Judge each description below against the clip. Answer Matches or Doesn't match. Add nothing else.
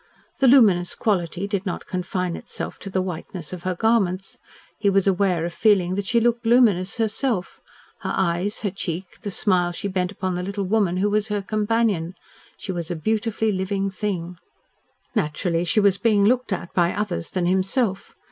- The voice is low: Doesn't match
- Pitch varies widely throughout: Doesn't match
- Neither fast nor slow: Matches